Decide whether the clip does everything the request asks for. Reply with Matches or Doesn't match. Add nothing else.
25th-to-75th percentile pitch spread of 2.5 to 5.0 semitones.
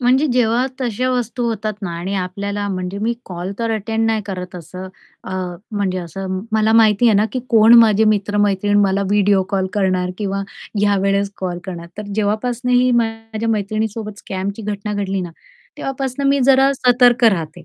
Matches